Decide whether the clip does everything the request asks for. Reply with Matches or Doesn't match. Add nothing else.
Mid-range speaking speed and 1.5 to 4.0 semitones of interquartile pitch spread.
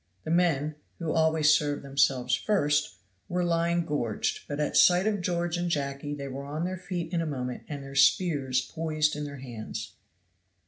Matches